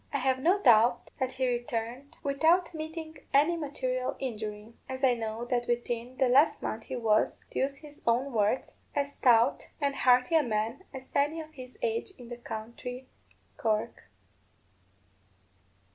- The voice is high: Yes, very high, 255 Hz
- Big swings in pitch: No, average, 3.2 semitones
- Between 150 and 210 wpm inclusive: Yes, average, 160 wpm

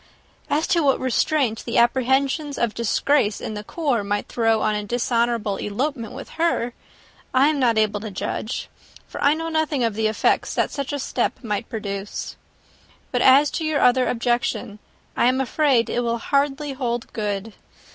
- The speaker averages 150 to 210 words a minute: Yes, average, 175 wpm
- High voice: Yes, high, 240 Hz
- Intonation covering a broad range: No, average, 4.3 semitones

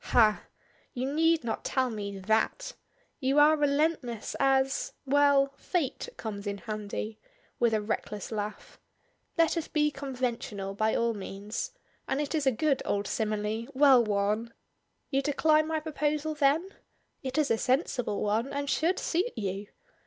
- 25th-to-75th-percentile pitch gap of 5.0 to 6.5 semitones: Yes, wide, 5.6 semitones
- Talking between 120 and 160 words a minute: Yes, average, 150 wpm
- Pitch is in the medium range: No, very high, 260 Hz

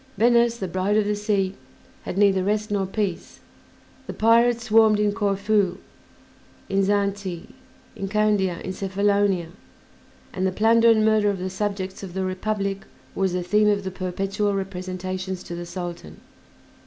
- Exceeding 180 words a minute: No, average, 155 wpm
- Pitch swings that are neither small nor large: No, narrow, 2.0 semitones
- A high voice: Yes, high, 195 Hz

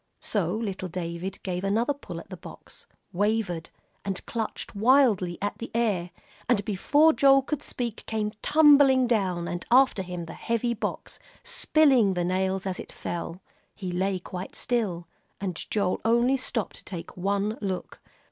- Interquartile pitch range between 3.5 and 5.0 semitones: Yes, average, 4.7 semitones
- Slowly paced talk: No, average, 155 wpm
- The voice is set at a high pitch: Yes, high, 205 Hz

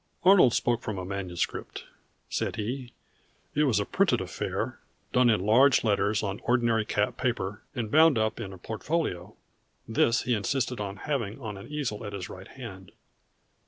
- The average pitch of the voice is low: Yes, low, 110 Hz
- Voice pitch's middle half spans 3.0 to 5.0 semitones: Yes, average, 4.0 semitones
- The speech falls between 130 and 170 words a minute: Yes, average, 165 wpm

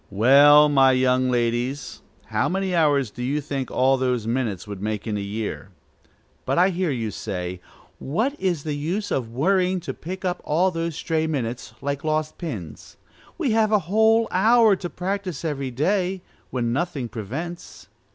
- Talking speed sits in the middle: Yes, average, 170 wpm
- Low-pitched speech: No, medium, 145 Hz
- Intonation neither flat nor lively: No, wide, 6.7 semitones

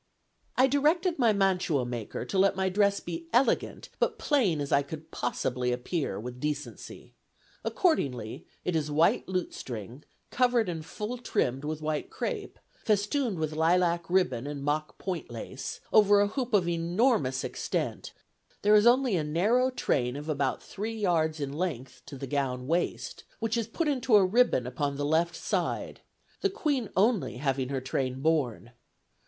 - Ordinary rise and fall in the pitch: No, wide, 7.5 semitones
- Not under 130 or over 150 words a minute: No, average, 160 wpm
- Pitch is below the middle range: No, medium, 170 Hz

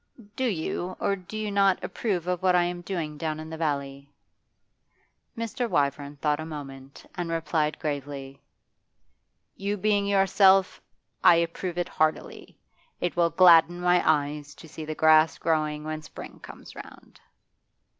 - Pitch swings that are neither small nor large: Yes, average, 3.5 semitones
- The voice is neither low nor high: Yes, medium, 165 Hz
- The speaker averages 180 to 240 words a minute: No, average, 150 wpm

